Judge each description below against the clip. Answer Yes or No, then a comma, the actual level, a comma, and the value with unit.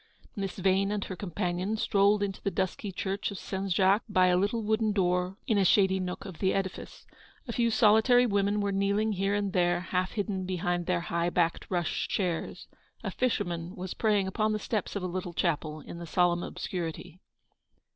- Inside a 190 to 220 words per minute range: Yes, average, 195 wpm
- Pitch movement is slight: Yes, narrow, 2.3 semitones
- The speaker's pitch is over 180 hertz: Yes, high, 190 Hz